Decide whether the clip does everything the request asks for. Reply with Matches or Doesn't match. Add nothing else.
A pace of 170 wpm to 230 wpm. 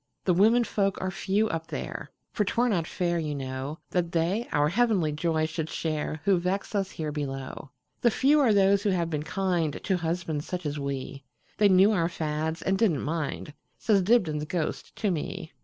Matches